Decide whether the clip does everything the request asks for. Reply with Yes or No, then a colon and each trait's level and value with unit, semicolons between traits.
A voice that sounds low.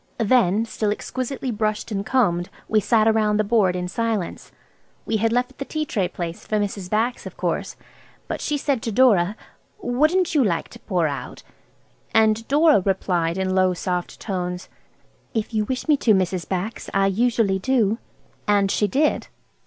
No: high, 215 Hz